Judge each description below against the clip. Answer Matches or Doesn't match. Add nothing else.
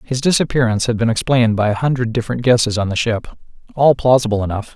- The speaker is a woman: Doesn't match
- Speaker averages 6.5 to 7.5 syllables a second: Matches